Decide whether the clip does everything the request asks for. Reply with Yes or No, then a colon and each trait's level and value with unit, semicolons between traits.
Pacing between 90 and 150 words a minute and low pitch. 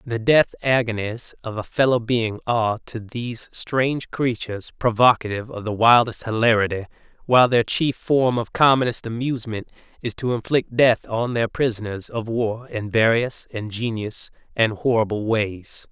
Yes: average, 145 wpm; low, 115 Hz